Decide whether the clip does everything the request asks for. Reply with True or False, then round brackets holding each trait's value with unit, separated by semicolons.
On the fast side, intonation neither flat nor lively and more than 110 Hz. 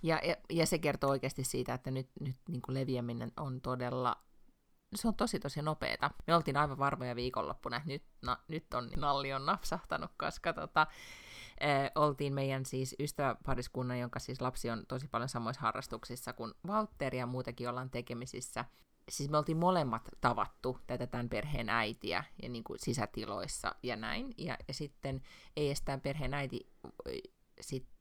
True (165 wpm; 3.3 semitones; 135 Hz)